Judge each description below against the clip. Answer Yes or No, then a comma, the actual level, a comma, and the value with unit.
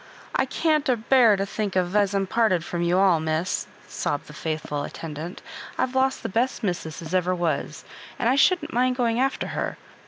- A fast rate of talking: Yes, fast, 210 wpm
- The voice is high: Yes, high, 195 Hz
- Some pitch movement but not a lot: No, wide, 6.7 semitones